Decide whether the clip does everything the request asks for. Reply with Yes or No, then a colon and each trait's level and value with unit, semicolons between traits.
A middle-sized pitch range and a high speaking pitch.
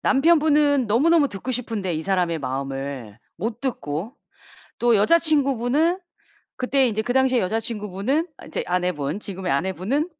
No: wide, 7.2 semitones; high, 225 Hz